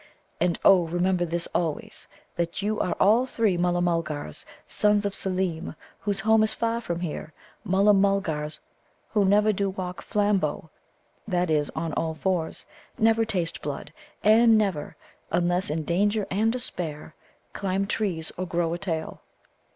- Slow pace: No, average, 150 wpm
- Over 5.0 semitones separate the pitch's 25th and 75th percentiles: No, average, 3.7 semitones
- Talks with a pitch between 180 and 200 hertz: Yes, medium, 185 Hz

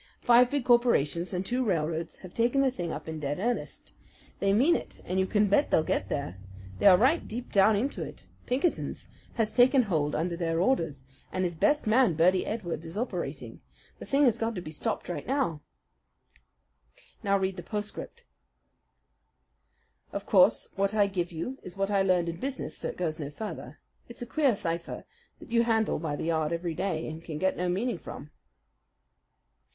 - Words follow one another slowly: No, average, 190 wpm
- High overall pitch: Yes, high, 195 Hz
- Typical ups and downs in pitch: No, wide, 6.1 semitones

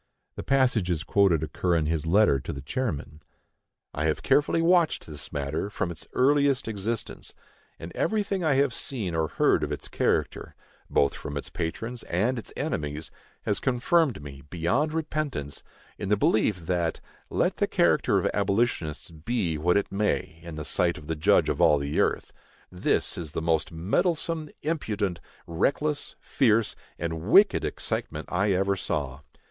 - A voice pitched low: Yes, very low, 95 Hz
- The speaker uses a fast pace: No, average, 160 wpm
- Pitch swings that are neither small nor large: No, wide, 8.2 semitones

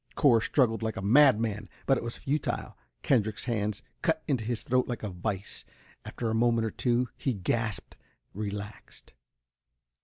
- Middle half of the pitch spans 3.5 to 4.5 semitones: No, average, 3.0 semitones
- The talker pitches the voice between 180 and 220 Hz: No, low, 115 Hz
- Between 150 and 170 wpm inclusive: Yes, average, 155 wpm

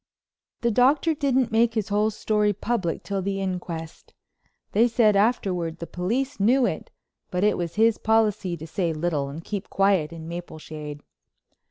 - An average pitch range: Yes, average, 4.9 semitones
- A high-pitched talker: Yes, high, 200 Hz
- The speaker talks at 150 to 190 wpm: Yes, average, 160 wpm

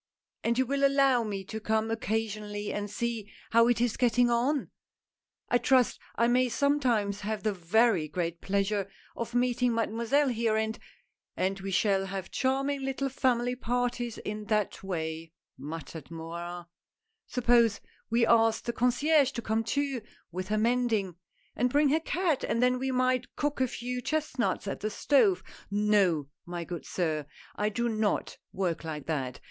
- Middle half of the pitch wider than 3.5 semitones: Yes, average, 4.2 semitones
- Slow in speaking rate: No, average, 170 wpm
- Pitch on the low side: No, high, 225 Hz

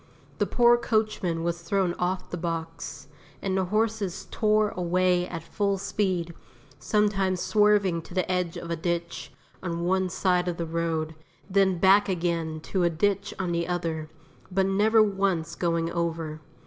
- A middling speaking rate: Yes, average, 160 wpm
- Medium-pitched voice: Yes, medium, 180 Hz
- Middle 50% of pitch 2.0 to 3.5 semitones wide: Yes, average, 2.7 semitones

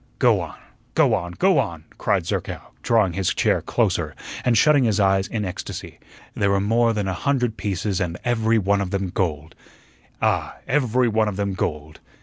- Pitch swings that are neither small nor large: Yes, average, 3.5 semitones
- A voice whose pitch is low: Yes, low, 100 Hz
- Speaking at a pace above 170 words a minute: Yes, average, 185 wpm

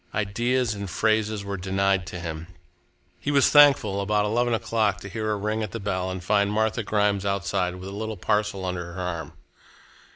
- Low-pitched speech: Yes, low, 100 Hz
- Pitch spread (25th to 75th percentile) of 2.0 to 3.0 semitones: Yes, average, 2.7 semitones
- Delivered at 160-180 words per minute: No, average, 190 wpm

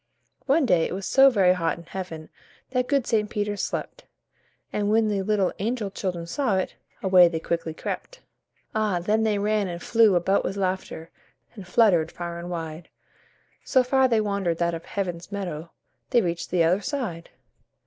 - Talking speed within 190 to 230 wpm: No, average, 180 wpm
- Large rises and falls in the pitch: No, average, 4.0 semitones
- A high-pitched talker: Yes, high, 195 Hz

